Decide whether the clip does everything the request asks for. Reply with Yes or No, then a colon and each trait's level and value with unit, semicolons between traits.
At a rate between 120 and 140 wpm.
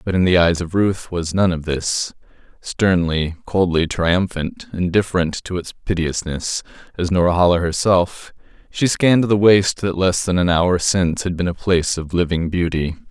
No: average, 165 wpm